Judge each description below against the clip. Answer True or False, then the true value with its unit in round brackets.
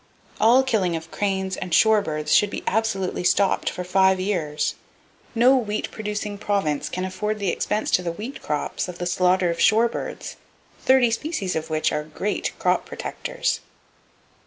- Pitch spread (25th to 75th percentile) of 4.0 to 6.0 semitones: False (3.6 semitones)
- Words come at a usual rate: True (165 wpm)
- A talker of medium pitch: False (195 Hz)